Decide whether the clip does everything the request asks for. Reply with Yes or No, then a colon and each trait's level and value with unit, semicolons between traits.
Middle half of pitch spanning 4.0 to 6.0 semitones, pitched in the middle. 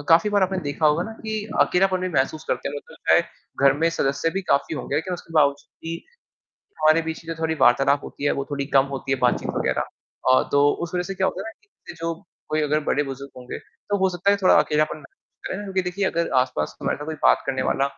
Yes: average, 4.3 semitones; medium, 160 Hz